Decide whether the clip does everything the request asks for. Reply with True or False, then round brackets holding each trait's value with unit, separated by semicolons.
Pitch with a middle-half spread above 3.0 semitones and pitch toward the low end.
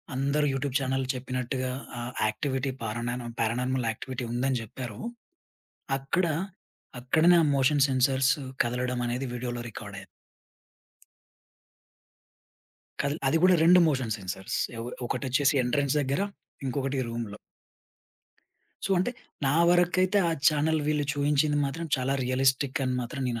False (2.7 semitones; 130 Hz)